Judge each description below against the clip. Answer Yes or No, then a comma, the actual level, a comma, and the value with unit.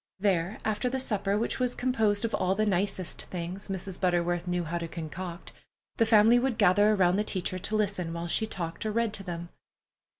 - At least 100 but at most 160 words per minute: No, average, 200 wpm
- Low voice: No, high, 195 Hz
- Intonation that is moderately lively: Yes, average, 3.5 semitones